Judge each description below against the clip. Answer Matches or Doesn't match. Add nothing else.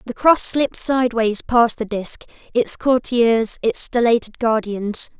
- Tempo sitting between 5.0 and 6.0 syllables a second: Doesn't match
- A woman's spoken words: Matches